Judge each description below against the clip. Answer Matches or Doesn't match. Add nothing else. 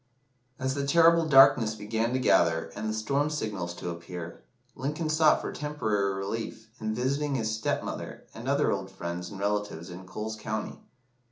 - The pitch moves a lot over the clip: Matches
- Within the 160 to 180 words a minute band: Matches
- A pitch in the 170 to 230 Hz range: Doesn't match